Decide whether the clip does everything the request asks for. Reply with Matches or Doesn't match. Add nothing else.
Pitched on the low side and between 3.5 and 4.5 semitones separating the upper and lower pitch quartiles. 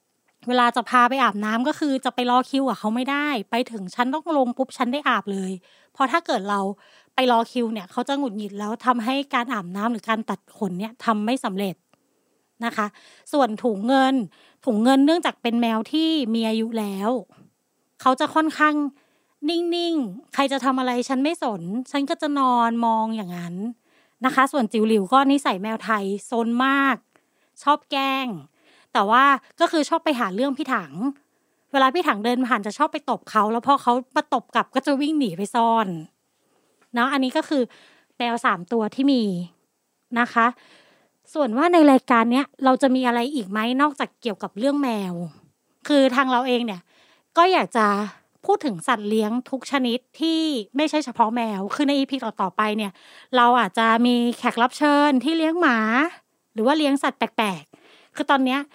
Doesn't match